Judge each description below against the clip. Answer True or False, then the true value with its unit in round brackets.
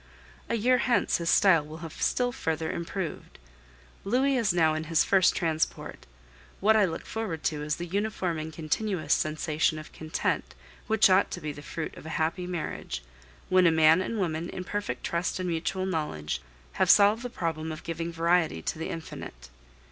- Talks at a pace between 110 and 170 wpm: False (185 wpm)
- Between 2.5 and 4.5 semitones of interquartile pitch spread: True (3.4 semitones)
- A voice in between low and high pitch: True (165 Hz)